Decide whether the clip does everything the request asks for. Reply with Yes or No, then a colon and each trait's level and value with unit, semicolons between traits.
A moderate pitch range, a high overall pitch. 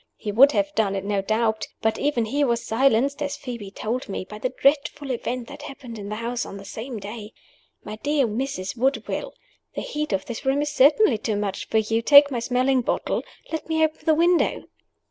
Yes: average, 4.6 semitones; high, 240 Hz